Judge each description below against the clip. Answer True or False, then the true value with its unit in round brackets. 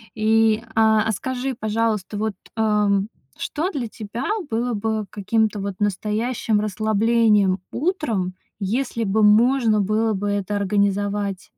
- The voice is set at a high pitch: True (215 Hz)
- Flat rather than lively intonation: True (1.9 semitones)